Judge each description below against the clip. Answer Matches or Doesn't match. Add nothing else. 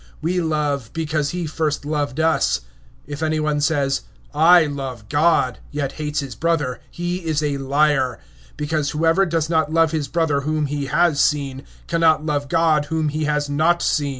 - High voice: Doesn't match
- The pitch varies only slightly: Matches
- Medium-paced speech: Matches